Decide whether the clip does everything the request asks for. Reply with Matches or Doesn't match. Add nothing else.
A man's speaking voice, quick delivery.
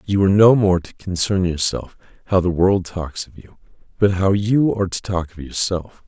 Matches